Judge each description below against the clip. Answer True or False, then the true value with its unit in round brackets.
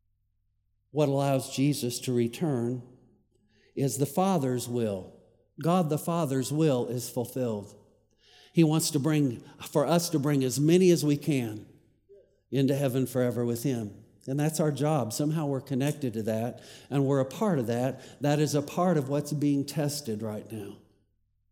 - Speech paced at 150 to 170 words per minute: True (160 wpm)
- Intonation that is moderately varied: True (4.7 semitones)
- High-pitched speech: False (130 Hz)